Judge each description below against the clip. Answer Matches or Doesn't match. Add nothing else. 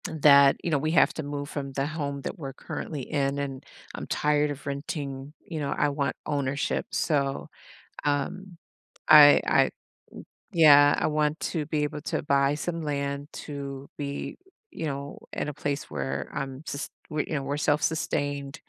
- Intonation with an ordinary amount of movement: Doesn't match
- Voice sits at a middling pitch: Matches